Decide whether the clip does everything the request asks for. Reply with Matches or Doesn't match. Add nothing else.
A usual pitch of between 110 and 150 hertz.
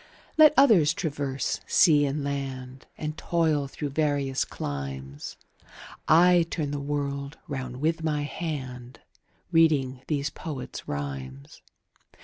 Matches